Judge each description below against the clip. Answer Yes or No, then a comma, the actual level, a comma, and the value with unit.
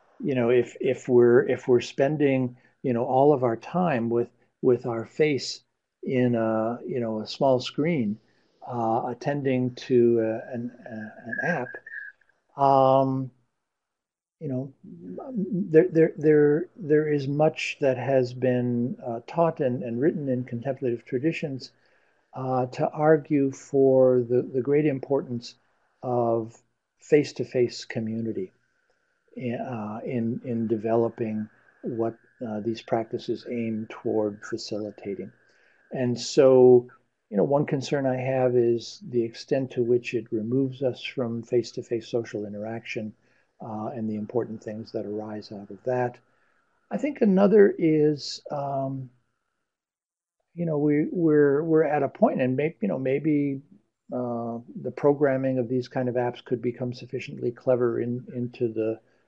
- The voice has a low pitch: Yes, low, 125 Hz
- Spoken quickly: No, average, 145 wpm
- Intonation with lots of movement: No, average, 3.2 semitones